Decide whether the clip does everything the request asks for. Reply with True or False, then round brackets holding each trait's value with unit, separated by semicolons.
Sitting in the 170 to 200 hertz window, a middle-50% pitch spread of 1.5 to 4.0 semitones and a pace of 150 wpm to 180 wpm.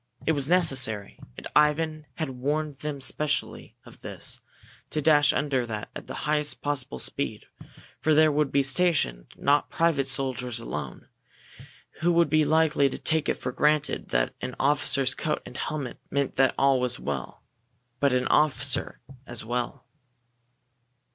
False (140 Hz; 3.1 semitones; 155 wpm)